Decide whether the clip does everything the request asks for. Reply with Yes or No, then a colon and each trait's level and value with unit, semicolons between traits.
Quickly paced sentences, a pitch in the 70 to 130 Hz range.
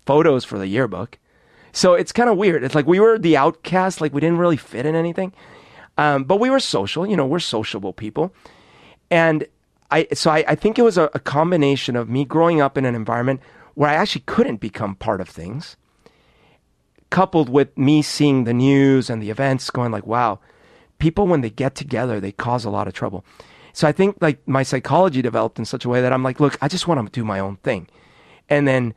No: fast, 220 wpm; medium, 140 Hz